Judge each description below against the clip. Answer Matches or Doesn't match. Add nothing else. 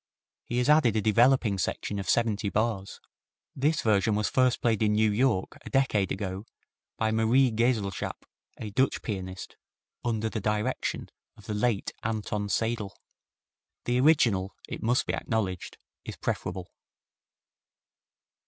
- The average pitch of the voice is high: Doesn't match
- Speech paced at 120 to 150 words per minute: Matches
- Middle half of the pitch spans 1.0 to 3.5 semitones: Matches